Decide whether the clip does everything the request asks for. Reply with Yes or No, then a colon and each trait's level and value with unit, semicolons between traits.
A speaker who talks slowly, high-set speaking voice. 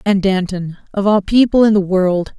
No: average, 200 wpm; high, 195 Hz